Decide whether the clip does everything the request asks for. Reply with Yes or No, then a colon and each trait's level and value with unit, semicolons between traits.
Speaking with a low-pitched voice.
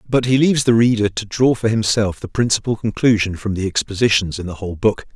Yes: low, 110 Hz